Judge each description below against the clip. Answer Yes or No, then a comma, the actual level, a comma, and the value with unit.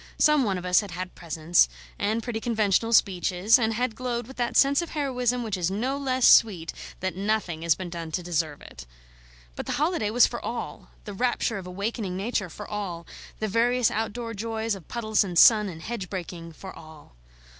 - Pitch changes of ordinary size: Yes, average, 4.8 semitones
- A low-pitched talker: No, high, 210 Hz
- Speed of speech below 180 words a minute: No, average, 200 wpm